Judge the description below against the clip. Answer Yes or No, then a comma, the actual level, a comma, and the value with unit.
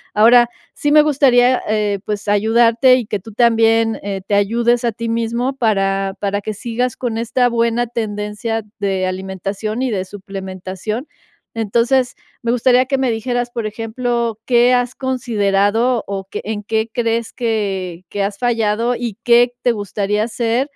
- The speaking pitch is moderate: No, high, 225 Hz